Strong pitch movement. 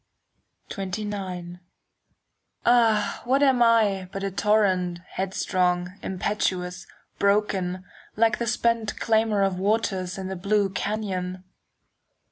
No: average, 2.8 semitones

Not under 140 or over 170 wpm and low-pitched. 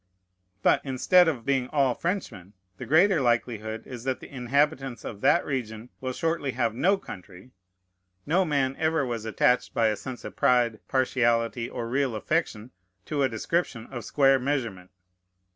Yes: average, 160 wpm; low, 125 Hz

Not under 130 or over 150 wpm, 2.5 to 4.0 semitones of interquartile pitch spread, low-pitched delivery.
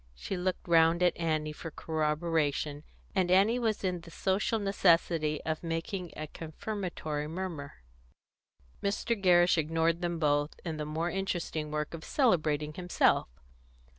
No: slow, 135 wpm; average, 3.1 semitones; medium, 165 Hz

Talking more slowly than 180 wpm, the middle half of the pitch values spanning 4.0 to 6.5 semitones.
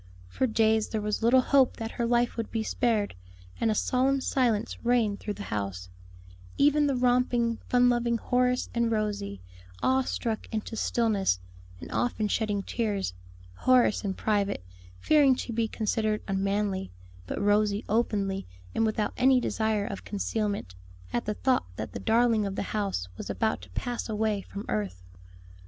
No: average, 160 wpm; average, 3.1 semitones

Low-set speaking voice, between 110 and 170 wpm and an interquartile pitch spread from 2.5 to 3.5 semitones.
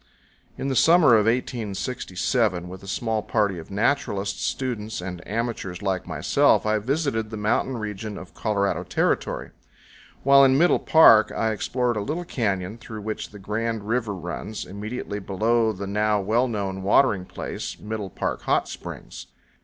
Yes: low, 110 Hz; average, 155 wpm; average, 3.2 semitones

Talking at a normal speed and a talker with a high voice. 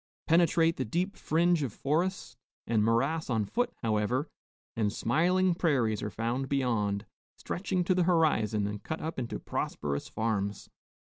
No: average, 145 wpm; low, 135 Hz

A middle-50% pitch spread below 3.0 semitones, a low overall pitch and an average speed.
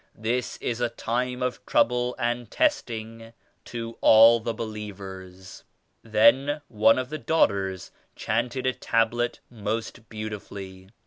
No: narrow, 2.4 semitones; low, 115 Hz; slow, 120 wpm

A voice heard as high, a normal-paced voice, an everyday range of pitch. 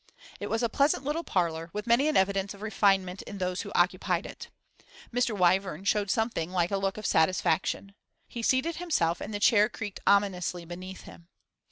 Yes: high, 200 Hz; average, 185 wpm; average, 3.6 semitones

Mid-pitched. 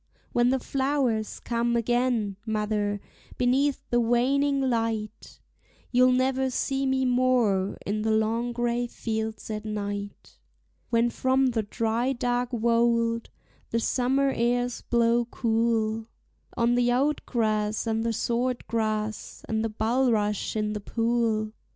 No: high, 235 Hz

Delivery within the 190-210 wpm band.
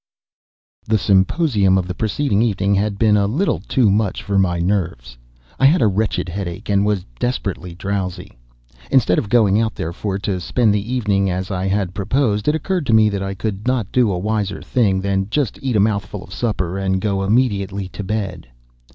Yes: average, 195 wpm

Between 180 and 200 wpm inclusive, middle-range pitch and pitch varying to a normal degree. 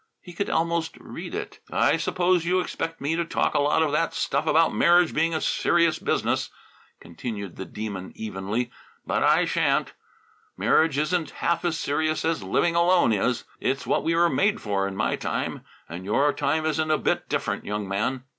No: average, 185 wpm; medium, 155 Hz; wide, 7.3 semitones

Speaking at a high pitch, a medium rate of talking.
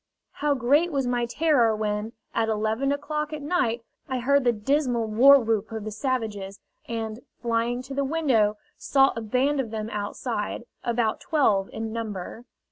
Yes: high, 235 Hz; average, 160 wpm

